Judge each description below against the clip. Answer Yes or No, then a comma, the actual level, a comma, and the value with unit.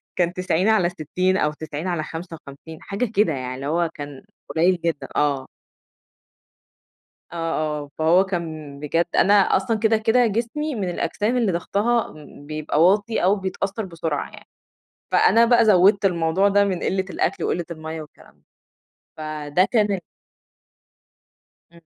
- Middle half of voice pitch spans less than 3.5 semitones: No, average, 4.3 semitones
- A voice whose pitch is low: No, medium, 175 Hz